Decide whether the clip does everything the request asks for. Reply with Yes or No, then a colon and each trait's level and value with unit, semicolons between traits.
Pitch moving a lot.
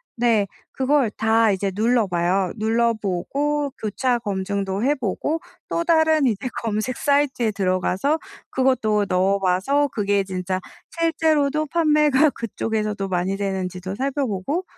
Yes: wide, 6.3 semitones